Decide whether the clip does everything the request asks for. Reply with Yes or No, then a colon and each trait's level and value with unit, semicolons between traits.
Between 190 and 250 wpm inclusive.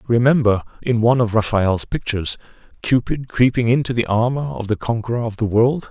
No: average, 175 wpm